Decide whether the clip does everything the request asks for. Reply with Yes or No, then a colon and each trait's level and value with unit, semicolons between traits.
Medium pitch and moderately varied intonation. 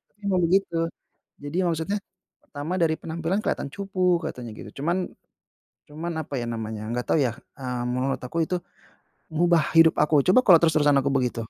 Yes: medium, 160 Hz; average, 4.4 semitones